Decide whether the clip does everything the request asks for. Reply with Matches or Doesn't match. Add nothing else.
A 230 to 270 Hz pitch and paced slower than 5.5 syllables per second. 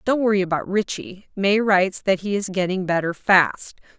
Doesn't match